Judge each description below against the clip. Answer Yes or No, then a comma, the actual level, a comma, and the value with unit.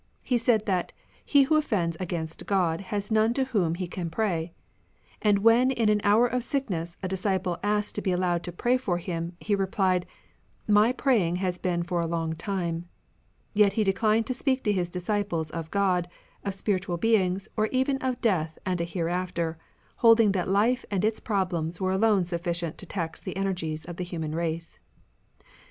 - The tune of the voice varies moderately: Yes, average, 3.9 semitones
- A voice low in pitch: No, high, 190 Hz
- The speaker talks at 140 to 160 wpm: No, average, 190 wpm